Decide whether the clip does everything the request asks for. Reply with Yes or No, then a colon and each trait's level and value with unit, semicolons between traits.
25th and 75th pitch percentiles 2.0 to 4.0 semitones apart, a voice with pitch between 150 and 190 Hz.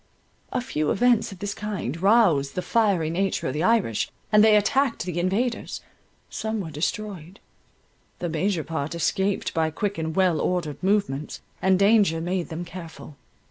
No: average, 4.4 semitones; medium, 185 Hz